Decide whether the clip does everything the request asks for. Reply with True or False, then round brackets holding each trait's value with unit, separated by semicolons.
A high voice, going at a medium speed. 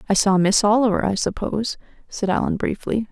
True (205 Hz; 175 wpm)